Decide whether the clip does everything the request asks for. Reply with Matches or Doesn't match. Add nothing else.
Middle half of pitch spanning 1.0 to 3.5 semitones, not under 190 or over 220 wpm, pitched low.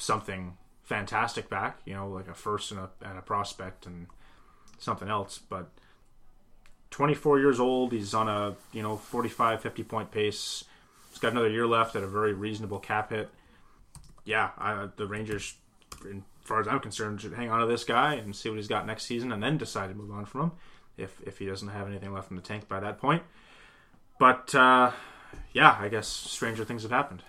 Matches